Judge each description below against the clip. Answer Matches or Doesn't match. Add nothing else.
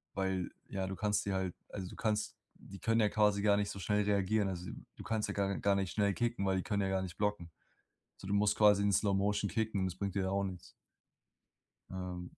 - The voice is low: Matches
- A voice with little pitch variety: Matches